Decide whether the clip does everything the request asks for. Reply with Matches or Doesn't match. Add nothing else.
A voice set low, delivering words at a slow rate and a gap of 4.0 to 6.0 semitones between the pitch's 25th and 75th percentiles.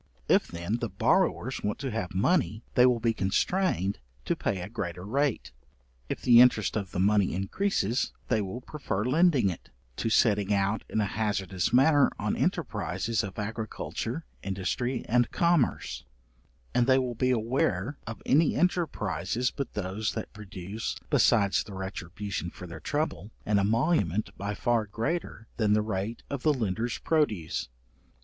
Doesn't match